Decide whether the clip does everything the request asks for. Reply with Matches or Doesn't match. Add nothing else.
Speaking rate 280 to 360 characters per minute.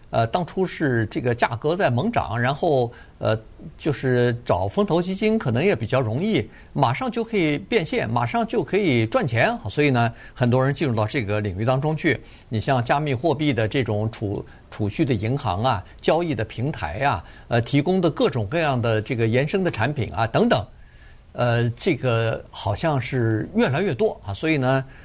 Doesn't match